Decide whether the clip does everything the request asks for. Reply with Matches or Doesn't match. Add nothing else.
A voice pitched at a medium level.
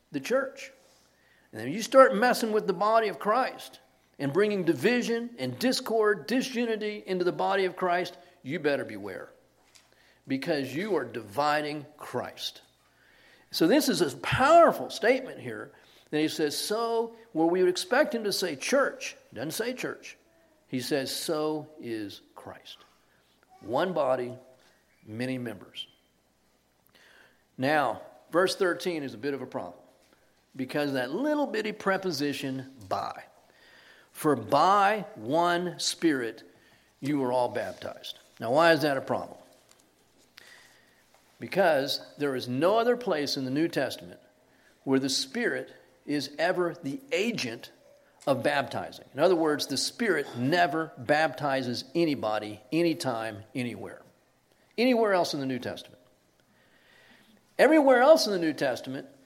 Matches